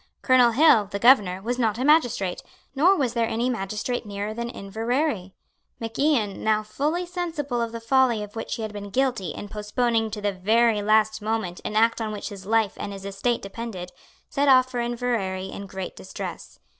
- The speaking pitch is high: Yes, high, 225 Hz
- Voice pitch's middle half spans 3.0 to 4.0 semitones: Yes, average, 3.4 semitones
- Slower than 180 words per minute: No, average, 195 wpm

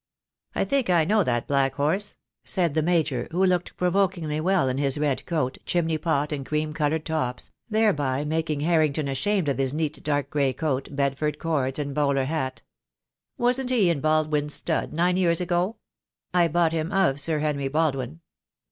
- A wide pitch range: No, average, 3.5 semitones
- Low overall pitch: No, medium, 155 Hz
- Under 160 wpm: No, average, 175 wpm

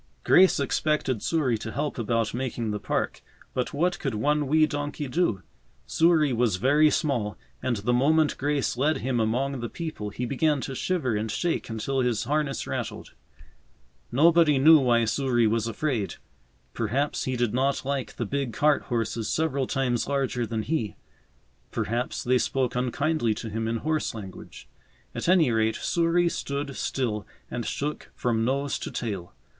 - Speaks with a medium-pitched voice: No, low, 130 Hz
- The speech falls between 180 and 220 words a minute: No, average, 160 wpm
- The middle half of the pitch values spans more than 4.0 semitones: Yes, average, 4.4 semitones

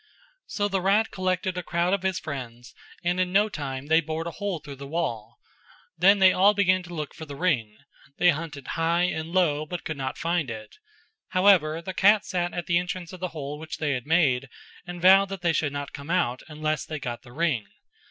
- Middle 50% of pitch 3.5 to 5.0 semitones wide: Yes, average, 4.2 semitones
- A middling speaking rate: No, fast, 220 wpm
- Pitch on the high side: No, medium, 165 Hz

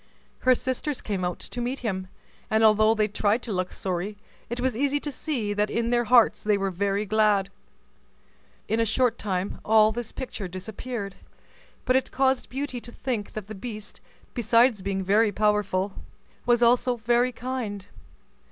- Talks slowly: No, average, 170 wpm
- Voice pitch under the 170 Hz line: No, high, 220 Hz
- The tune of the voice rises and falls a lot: No, average, 3.4 semitones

